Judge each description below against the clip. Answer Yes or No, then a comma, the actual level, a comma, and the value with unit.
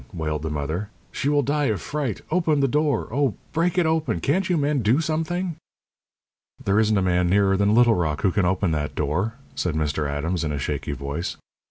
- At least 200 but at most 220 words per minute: Yes, fast, 205 wpm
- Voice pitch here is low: Yes, low, 105 Hz